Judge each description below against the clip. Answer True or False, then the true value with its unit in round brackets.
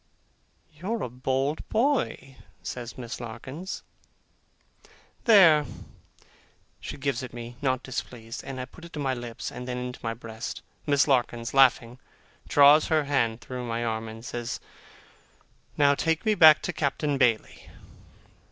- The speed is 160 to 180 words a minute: False (145 wpm)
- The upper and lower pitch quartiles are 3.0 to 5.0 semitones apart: True (3.7 semitones)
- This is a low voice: True (130 Hz)